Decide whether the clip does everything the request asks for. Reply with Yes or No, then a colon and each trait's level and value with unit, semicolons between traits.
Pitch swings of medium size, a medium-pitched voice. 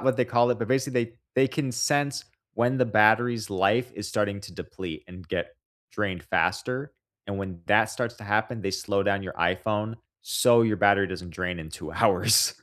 No: average, 3.9 semitones; low, 110 Hz